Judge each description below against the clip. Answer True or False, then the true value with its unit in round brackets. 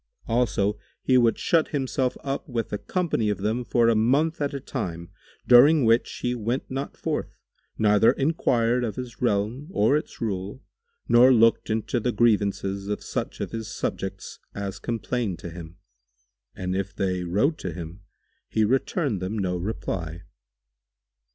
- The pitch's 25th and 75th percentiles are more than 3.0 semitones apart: True (4.2 semitones)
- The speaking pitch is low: True (115 Hz)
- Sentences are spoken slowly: False (155 wpm)